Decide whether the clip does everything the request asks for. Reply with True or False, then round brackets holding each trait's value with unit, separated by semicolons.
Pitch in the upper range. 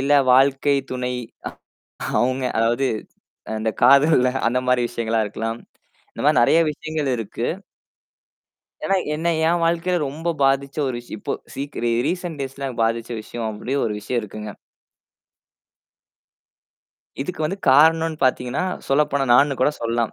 False (135 Hz)